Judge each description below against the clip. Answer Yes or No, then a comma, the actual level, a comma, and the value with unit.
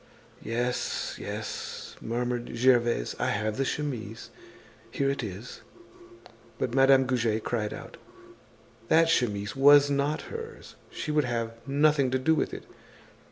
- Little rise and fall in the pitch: No, average, 3.5 semitones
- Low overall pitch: Yes, low, 125 Hz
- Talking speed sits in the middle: No, slow, 130 wpm